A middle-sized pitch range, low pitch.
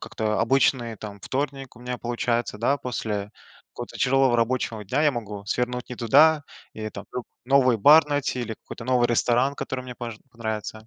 Yes: average, 3.0 semitones; low, 120 Hz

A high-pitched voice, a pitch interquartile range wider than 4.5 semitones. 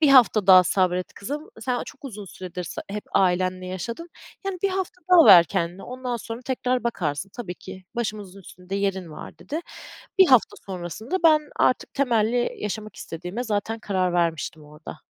Yes: high, 205 Hz; average, 5.3 semitones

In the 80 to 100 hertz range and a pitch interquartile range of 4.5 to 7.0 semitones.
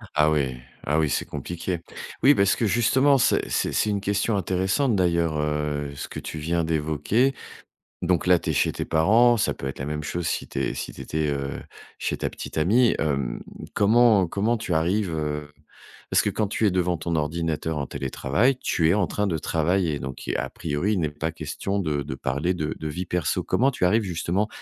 Yes: very low, 85 Hz; average, 5.0 semitones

